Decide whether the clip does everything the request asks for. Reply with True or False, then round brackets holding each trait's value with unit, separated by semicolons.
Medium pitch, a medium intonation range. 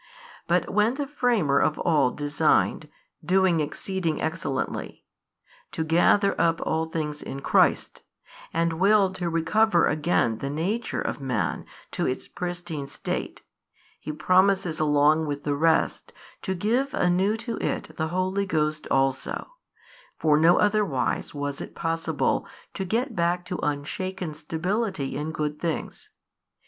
True (165 Hz; 4.1 semitones)